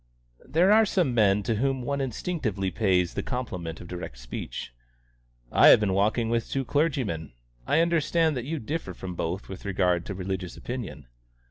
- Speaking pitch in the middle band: No, low, 110 Hz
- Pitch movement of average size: No, wide, 7.1 semitones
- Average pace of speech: Yes, average, 170 wpm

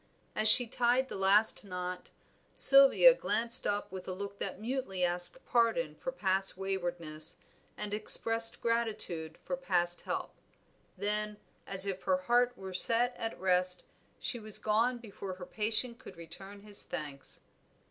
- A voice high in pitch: Yes, high, 200 Hz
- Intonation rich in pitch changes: No, average, 4.1 semitones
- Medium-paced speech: Yes, average, 145 wpm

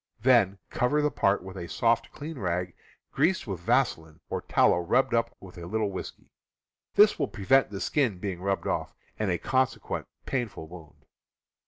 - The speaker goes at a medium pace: Yes, average, 170 wpm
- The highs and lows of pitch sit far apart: Yes, wide, 5.7 semitones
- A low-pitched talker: Yes, low, 100 Hz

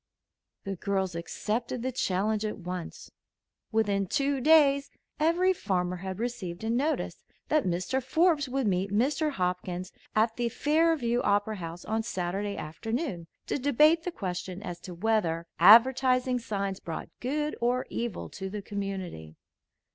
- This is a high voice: Yes, high, 220 Hz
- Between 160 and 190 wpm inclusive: No, average, 140 wpm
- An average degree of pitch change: No, wide, 6.0 semitones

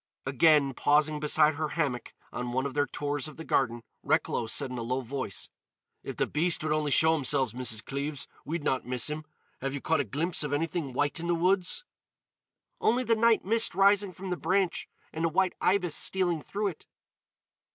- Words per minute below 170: No, average, 195 wpm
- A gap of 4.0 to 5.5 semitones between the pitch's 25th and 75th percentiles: Yes, average, 4.4 semitones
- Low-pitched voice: No, medium, 150 Hz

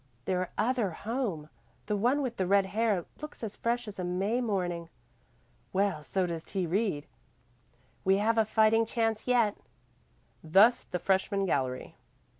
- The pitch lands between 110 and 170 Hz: No, high, 200 Hz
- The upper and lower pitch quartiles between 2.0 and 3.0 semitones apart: No, average, 3.8 semitones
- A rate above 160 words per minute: No, average, 150 wpm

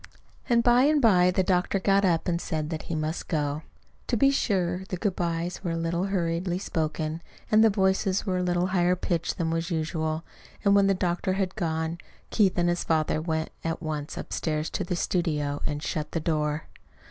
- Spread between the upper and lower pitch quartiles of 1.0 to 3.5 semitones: Yes, average, 3.1 semitones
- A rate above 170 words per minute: Yes, fast, 205 wpm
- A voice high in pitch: No, medium, 175 Hz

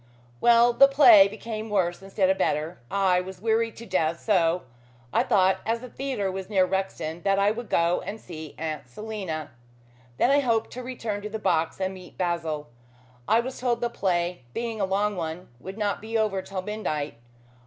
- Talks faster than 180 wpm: Yes, average, 190 wpm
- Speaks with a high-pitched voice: Yes, high, 195 Hz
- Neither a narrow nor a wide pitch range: Yes, average, 4.0 semitones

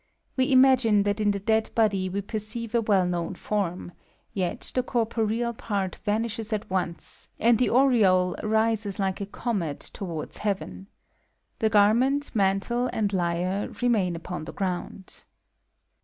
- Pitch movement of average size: Yes, average, 3.4 semitones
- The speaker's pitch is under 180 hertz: No, high, 205 Hz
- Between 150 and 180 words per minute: No, average, 140 wpm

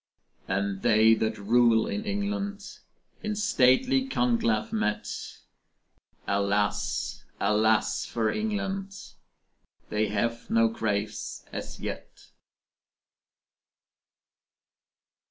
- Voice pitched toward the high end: No, low, 115 Hz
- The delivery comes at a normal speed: No, slow, 80 wpm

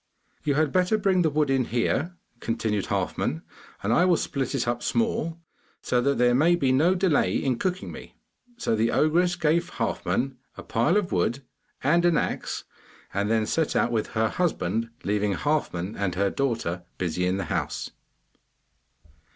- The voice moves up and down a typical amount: No, wide, 7.3 semitones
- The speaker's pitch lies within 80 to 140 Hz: Yes, low, 135 Hz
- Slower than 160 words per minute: No, average, 170 wpm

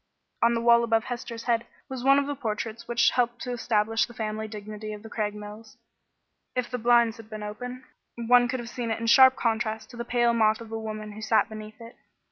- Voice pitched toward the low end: No, high, 230 Hz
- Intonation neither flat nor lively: No, narrow, 1.8 semitones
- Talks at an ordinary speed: No, fast, 225 wpm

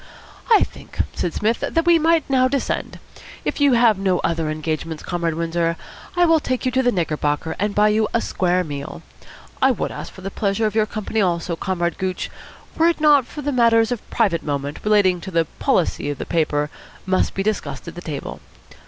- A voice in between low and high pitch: No, high, 195 Hz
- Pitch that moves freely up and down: Yes, wide, 6.4 semitones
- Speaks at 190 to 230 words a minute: Yes, average, 200 wpm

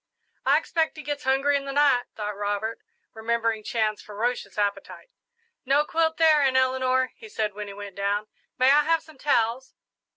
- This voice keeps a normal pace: Yes, average, 175 wpm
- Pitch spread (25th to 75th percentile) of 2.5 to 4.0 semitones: No, average, 5.2 semitones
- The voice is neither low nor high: No, very high, 255 Hz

